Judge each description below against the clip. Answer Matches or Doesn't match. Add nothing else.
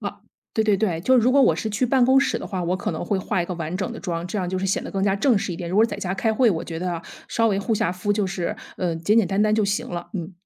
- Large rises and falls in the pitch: Doesn't match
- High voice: Matches